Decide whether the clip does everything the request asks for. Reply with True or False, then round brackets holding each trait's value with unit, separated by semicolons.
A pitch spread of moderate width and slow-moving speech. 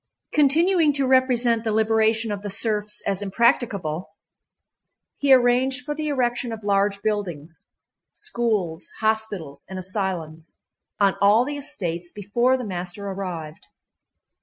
True (4.7 semitones; 115 wpm)